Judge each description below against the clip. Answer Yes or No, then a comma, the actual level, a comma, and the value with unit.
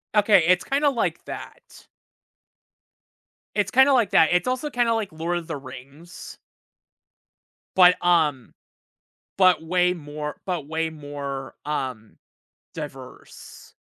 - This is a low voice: No, medium, 170 Hz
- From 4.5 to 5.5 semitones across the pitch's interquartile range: Yes, average, 5.2 semitones